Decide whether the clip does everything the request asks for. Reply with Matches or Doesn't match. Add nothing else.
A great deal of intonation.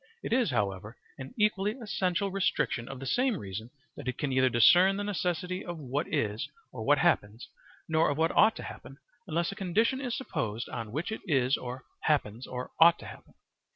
Matches